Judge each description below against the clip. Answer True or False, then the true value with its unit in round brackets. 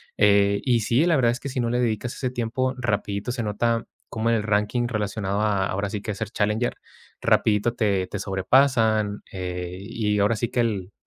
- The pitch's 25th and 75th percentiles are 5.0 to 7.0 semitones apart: False (2.8 semitones)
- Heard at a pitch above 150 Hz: False (110 Hz)